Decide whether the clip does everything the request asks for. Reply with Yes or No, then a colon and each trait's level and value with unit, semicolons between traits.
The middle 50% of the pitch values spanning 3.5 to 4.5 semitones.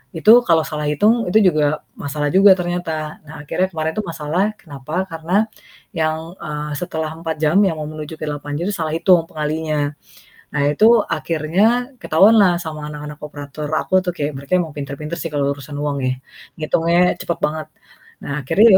No: average, 2.9 semitones